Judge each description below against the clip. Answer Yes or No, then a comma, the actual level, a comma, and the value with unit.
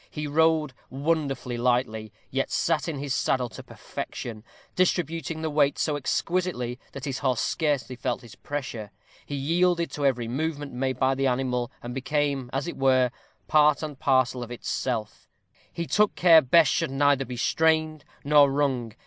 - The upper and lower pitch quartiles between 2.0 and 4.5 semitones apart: Yes, average, 3.7 semitones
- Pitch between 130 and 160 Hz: Yes, medium, 140 Hz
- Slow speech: No, average, 160 wpm